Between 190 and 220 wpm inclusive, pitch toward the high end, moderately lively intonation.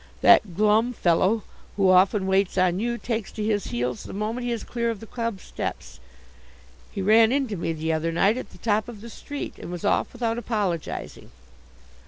Yes: average, 195 wpm; high, 210 Hz; average, 3.9 semitones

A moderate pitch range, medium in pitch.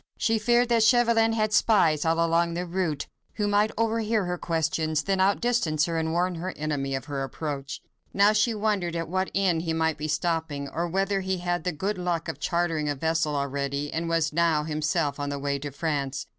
Yes: average, 4.4 semitones; medium, 165 Hz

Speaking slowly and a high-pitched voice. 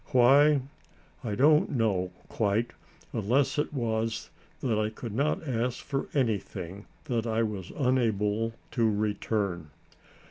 No: slow, 120 wpm; low, 115 Hz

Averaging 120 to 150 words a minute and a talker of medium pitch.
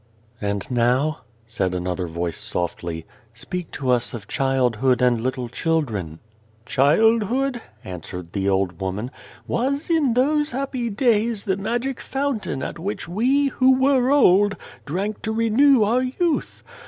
Yes: average, 145 wpm; medium, 170 Hz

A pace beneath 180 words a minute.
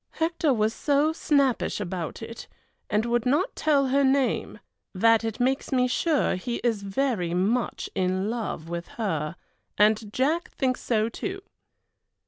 Yes: average, 145 wpm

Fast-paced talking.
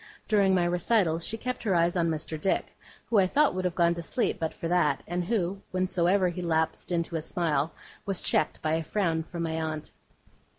Yes: fast, 210 wpm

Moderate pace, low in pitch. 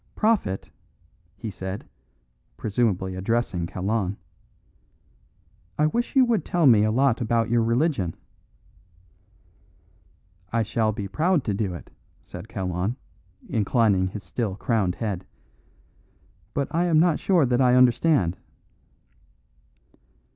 No: slow, 115 wpm; low, 115 Hz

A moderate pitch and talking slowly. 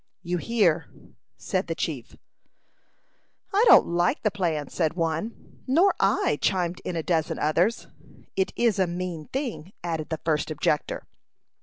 No: medium, 175 Hz; average, 145 wpm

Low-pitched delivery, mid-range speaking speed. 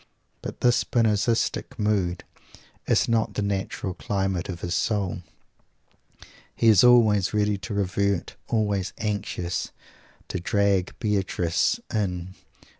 No: low, 100 Hz; slow, 115 wpm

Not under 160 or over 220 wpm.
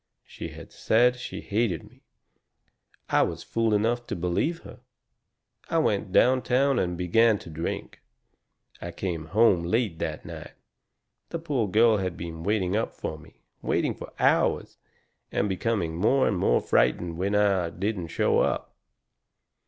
No: average, 150 wpm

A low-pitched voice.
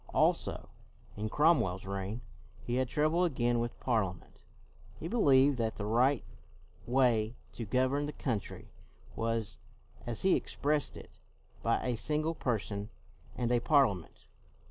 Yes: low, 120 Hz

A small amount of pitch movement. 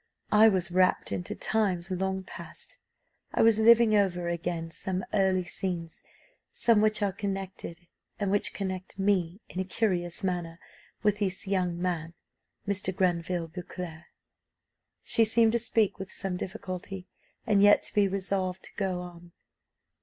Yes: narrow, 2.3 semitones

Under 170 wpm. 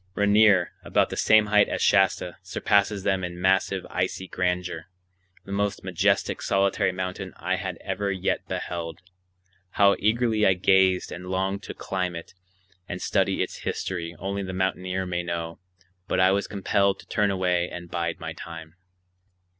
Yes: average, 160 wpm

